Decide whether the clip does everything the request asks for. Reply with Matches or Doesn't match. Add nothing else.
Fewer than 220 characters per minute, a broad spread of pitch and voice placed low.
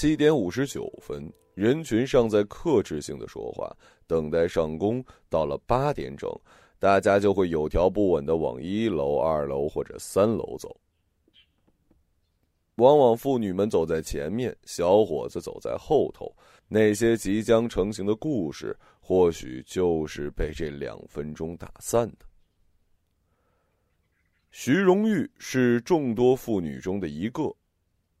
Matches